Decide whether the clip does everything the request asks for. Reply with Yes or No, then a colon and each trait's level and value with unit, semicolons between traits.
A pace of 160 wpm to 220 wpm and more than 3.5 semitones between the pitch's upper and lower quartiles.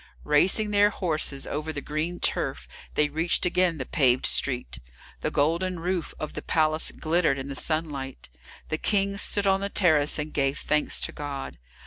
Yes: average, 170 wpm; average, 3.9 semitones